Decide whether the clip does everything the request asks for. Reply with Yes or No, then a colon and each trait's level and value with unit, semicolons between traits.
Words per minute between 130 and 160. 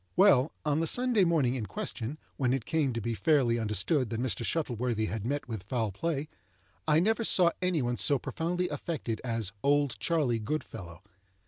No: average, 180 wpm